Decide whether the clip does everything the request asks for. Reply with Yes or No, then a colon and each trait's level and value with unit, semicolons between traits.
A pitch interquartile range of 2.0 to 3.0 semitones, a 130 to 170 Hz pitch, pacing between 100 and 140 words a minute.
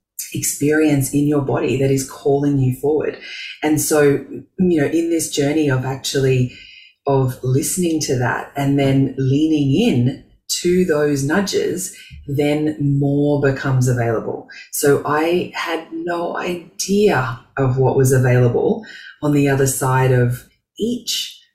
Yes: narrow, 2.6 semitones; medium, 140 Hz; slow, 135 wpm